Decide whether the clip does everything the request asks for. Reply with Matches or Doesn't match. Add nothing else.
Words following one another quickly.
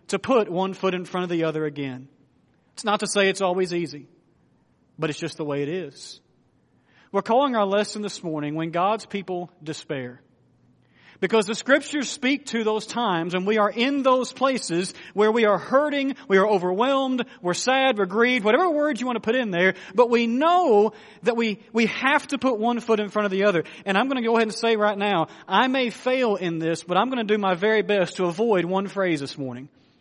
Matches